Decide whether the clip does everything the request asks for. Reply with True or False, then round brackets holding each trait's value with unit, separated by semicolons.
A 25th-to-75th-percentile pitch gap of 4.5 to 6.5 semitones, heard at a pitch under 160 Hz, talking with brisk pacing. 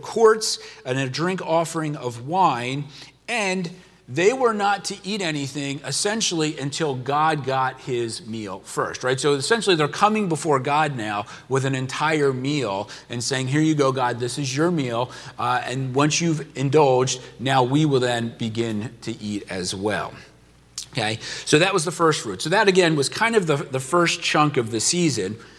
False (4.8 semitones; 140 Hz; 180 wpm)